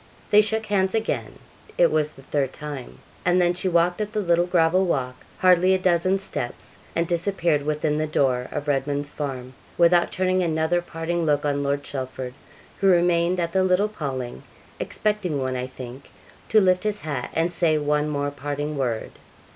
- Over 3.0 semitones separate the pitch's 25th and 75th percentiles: Yes, average, 4.2 semitones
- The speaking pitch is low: No, medium, 165 Hz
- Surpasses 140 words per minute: Yes, average, 180 wpm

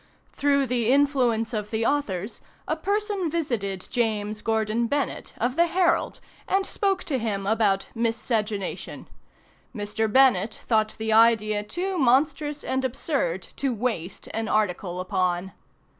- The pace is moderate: No, slow, 130 wpm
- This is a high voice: Yes, high, 230 Hz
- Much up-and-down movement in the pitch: No, average, 5.0 semitones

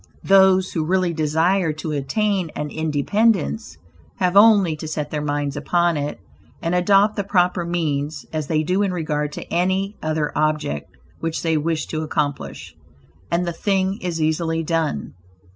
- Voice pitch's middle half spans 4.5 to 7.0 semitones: No, average, 3.5 semitones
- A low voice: No, medium, 165 Hz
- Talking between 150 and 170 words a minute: Yes, average, 160 wpm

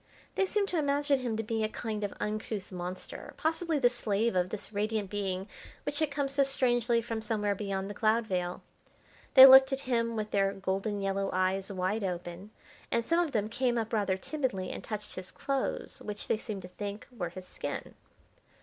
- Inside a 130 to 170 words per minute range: No, average, 195 wpm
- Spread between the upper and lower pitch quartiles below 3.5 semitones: No, average, 4.2 semitones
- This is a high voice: Yes, high, 215 Hz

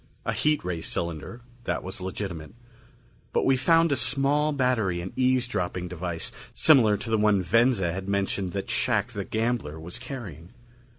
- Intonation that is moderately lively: No, wide, 5.9 semitones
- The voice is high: No, low, 105 Hz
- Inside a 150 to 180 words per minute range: Yes, average, 160 wpm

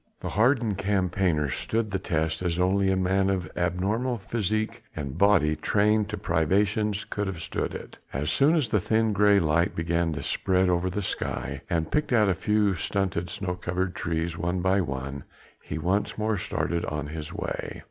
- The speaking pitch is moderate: No, very low, 95 Hz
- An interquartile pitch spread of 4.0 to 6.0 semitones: No, average, 3.6 semitones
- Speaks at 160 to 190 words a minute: Yes, average, 180 wpm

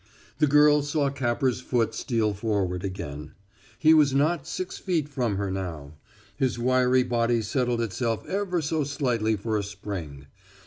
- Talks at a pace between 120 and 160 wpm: Yes, average, 150 wpm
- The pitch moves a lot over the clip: Yes, wide, 5.9 semitones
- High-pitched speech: No, low, 120 Hz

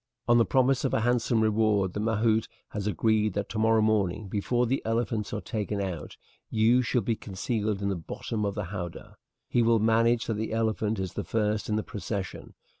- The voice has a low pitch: Yes, low, 110 Hz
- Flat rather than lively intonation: Yes, narrow, 1.9 semitones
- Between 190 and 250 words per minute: Yes, average, 195 wpm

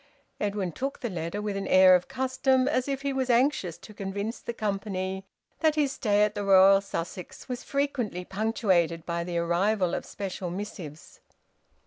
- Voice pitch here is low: No, high, 200 Hz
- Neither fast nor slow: Yes, average, 170 wpm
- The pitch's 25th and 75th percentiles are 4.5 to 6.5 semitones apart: Yes, average, 5.0 semitones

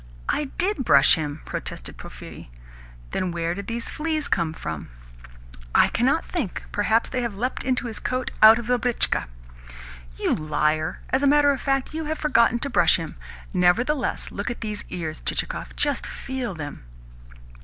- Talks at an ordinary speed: Yes, average, 165 wpm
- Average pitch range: No, wide, 7.8 semitones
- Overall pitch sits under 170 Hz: No, high, 235 Hz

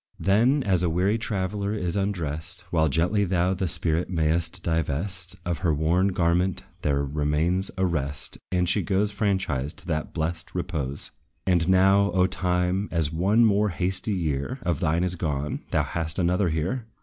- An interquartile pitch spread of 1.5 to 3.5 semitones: Yes, average, 3.2 semitones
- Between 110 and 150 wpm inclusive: No, average, 165 wpm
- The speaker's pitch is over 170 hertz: No, very low, 90 Hz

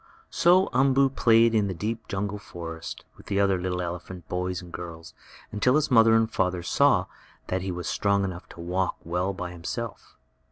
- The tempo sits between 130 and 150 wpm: No, average, 185 wpm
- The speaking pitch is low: Yes, very low, 95 Hz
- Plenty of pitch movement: No, average, 4.2 semitones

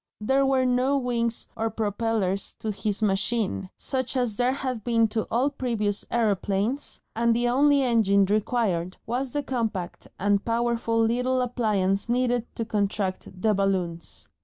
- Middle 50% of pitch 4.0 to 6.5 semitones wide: No, average, 3.4 semitones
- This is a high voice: Yes, high, 230 Hz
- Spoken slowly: No, average, 145 wpm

